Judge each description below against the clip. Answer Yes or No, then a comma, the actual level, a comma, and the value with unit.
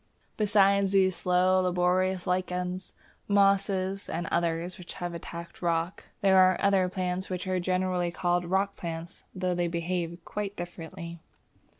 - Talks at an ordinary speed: No, slow, 130 wpm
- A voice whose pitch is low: No, medium, 180 Hz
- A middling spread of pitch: No, narrow, 1.5 semitones